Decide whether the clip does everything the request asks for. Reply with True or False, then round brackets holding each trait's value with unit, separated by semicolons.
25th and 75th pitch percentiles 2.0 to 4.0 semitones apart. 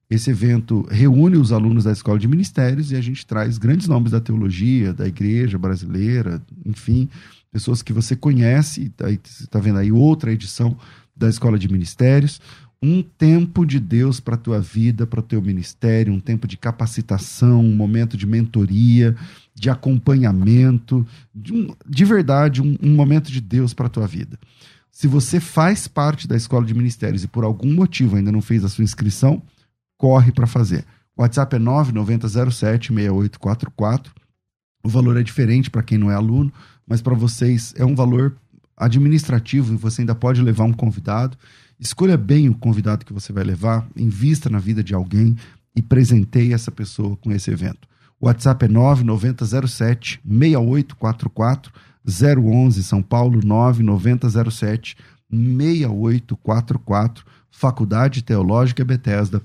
True (3.3 semitones)